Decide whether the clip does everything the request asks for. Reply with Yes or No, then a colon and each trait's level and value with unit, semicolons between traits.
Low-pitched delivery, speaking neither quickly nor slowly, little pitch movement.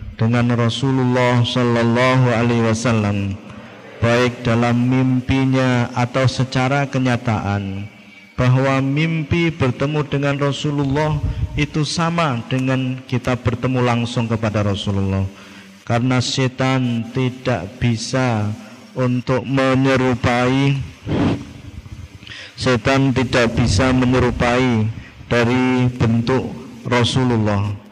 No: low, 125 Hz; slow, 80 wpm; narrow, 2.3 semitones